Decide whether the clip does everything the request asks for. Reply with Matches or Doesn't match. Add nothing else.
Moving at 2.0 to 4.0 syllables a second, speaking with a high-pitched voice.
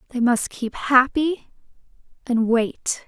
Matches